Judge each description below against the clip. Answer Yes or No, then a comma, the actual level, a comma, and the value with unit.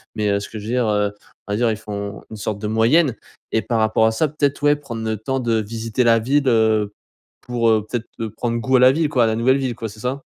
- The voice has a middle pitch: No, low, 115 Hz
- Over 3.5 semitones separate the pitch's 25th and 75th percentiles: No, average, 2.7 semitones